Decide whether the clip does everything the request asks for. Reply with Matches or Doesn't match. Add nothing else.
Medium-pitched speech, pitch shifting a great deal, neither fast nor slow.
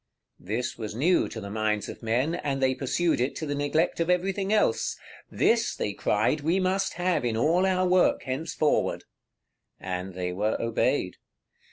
Matches